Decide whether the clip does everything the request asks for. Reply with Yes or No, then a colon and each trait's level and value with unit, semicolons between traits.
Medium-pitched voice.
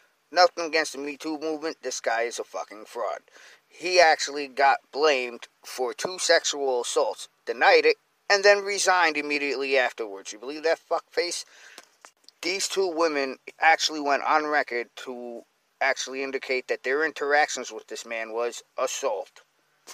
Yes: medium, 150 Hz